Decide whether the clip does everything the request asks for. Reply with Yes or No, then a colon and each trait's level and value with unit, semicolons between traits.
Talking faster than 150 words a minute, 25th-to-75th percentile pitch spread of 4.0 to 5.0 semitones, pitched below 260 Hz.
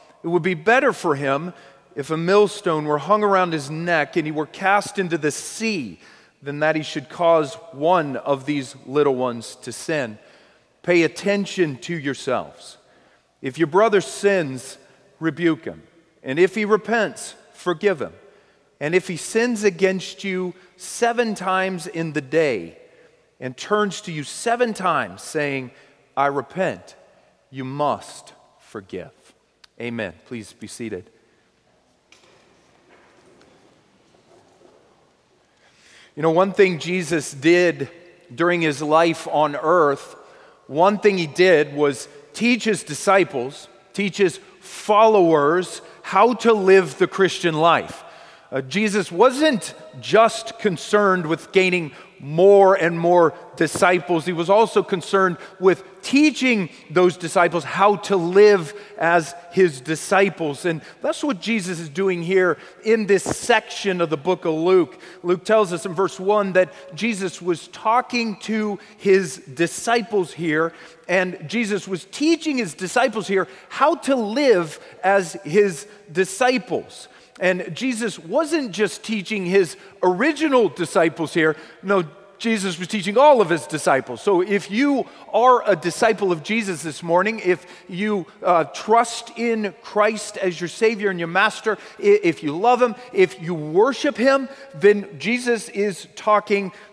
No: slow, 135 wpm; average, 4.3 semitones; medium, 185 Hz